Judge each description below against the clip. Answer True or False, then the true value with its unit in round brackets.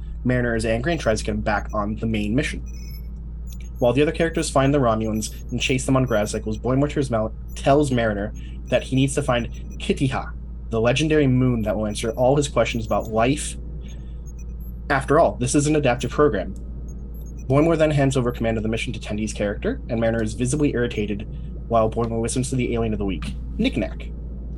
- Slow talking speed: False (195 wpm)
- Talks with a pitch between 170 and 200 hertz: False (115 Hz)